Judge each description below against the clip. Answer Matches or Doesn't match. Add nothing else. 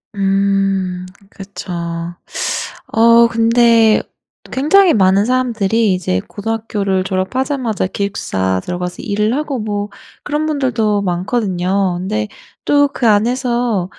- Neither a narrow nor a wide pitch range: Matches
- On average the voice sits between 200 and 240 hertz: Matches